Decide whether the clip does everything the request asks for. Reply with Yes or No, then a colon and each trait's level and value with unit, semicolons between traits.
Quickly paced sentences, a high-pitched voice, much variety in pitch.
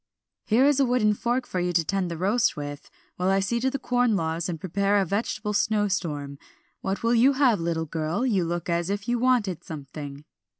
Yes: fast, 210 wpm; high, 195 Hz; wide, 6.0 semitones